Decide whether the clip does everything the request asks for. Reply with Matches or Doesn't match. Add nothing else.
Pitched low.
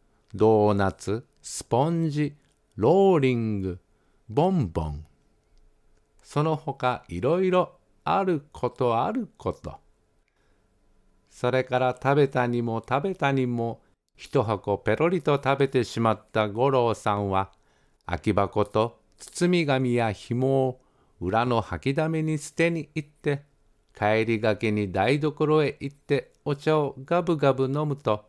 Matches